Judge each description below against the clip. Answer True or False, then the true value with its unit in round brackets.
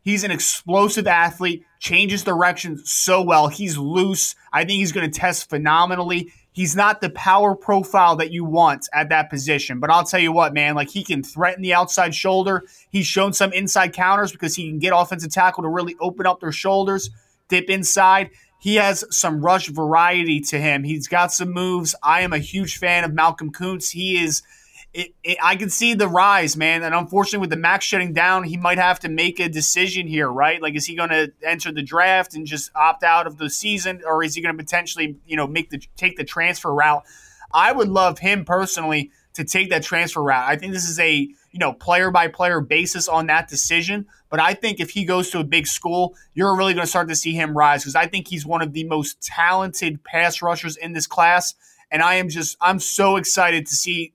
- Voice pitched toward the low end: False (175 Hz)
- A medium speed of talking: False (220 wpm)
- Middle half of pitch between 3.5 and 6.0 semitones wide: False (2.8 semitones)